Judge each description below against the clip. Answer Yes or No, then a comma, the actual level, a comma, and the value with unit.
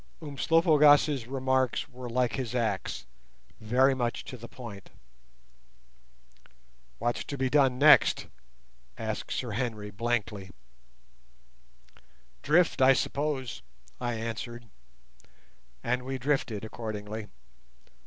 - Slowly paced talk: Yes, slow, 95 wpm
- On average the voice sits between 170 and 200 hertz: No, low, 125 Hz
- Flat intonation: No, average, 3.0 semitones